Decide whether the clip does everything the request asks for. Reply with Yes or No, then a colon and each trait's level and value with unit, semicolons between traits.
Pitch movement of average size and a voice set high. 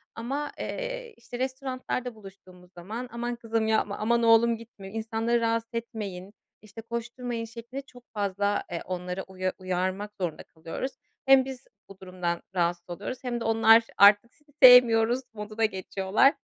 Yes: average, 3.9 semitones; high, 225 Hz